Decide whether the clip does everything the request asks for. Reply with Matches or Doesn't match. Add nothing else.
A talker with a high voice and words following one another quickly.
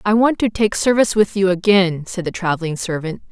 Matches